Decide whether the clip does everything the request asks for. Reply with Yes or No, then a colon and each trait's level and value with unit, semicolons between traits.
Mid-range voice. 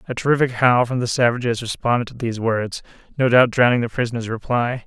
No: low, 120 Hz